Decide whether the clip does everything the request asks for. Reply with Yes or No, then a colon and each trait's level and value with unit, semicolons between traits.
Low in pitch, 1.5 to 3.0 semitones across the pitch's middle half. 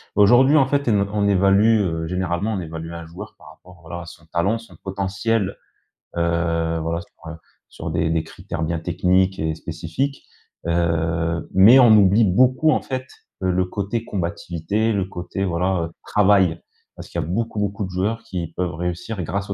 No: very low, 95 Hz; average, 3.7 semitones